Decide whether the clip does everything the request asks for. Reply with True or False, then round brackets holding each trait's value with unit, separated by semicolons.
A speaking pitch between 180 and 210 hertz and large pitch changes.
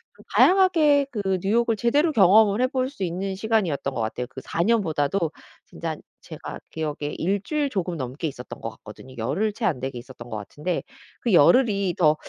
True (190 Hz; 7.9 semitones)